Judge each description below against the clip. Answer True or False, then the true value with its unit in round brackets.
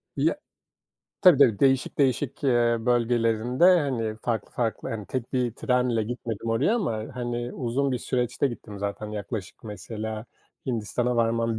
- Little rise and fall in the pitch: True (2.1 semitones)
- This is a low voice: True (120 Hz)